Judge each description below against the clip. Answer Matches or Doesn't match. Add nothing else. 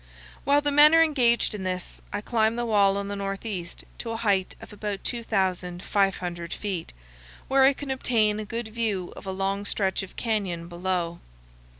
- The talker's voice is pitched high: Matches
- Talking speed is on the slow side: Doesn't match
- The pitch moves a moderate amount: Matches